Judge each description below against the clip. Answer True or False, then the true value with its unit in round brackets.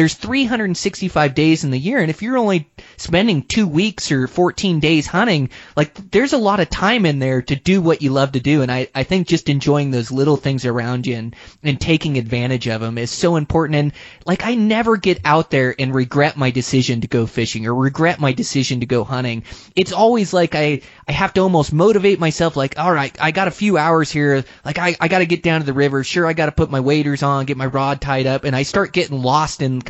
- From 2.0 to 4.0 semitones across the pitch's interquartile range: False (5.0 semitones)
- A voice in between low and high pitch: True (150 Hz)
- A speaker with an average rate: False (245 wpm)